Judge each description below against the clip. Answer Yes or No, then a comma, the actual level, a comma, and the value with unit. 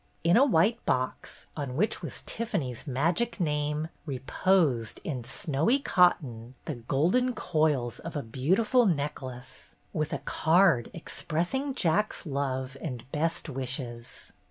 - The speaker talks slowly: Yes, slow, 130 wpm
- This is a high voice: No, medium, 150 Hz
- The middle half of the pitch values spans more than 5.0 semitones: Yes, wide, 5.4 semitones